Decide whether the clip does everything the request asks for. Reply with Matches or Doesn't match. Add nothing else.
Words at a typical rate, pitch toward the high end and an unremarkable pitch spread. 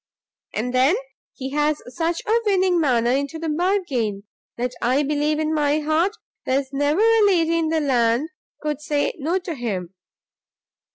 Matches